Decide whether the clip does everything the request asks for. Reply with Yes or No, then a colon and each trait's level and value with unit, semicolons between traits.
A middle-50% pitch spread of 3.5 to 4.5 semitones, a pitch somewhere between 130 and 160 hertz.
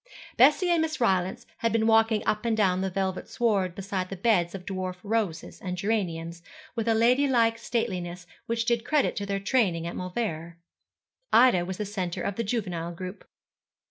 No: average, 4.0 semitones; high, 200 Hz